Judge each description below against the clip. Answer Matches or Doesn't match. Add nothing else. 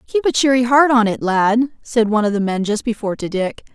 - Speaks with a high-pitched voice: Matches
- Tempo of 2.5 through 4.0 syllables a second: Doesn't match